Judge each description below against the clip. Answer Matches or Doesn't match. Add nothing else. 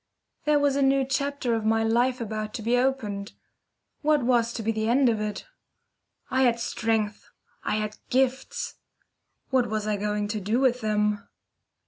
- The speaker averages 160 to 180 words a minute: Matches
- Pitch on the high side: Matches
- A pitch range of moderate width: Matches